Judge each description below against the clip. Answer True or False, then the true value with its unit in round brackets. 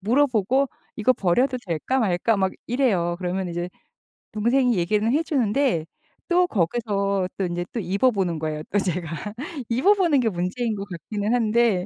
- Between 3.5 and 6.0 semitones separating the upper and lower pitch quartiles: True (5.5 semitones)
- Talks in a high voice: True (205 Hz)